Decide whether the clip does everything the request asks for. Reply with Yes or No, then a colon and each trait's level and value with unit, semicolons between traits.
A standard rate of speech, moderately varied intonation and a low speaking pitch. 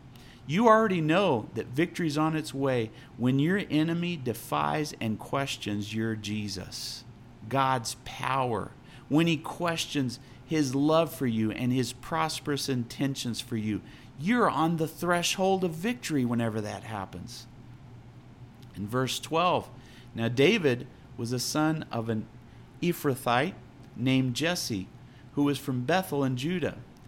No: slow, 130 wpm; average, 4.4 semitones; low, 130 Hz